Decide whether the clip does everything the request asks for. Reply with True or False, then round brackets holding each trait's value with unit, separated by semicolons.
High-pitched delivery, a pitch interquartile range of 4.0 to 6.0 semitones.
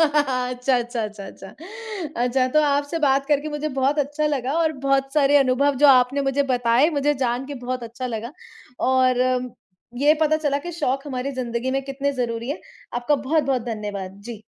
False (270 Hz; 2.7 semitones)